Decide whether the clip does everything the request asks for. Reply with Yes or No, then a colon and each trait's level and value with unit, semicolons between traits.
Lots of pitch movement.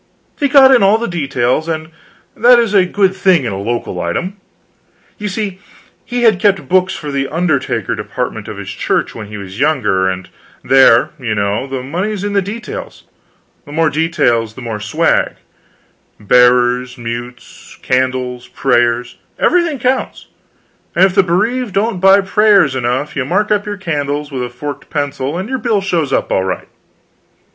Yes: wide, 8.1 semitones